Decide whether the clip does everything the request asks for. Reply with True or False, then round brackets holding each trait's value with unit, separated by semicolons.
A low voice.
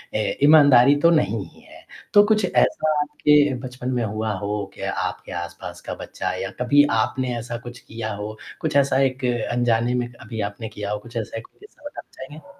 True (120 Hz)